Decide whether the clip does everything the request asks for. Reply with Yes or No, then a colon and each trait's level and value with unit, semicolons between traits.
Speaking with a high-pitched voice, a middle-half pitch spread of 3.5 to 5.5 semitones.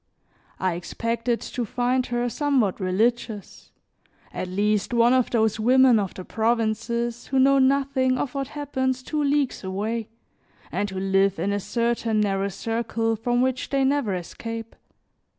Yes: high, 230 Hz; average, 3.9 semitones